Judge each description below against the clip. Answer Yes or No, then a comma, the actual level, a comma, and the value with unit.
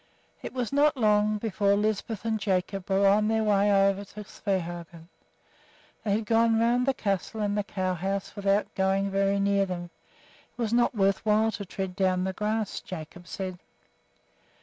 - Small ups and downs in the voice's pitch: Yes, narrow, 2.1 semitones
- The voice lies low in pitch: No, high, 200 Hz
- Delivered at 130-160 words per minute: No, average, 170 wpm